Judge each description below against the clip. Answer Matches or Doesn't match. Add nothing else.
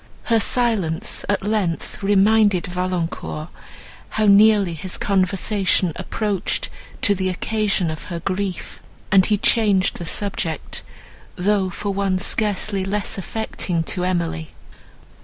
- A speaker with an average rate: Doesn't match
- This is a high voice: Matches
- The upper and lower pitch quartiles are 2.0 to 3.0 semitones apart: Matches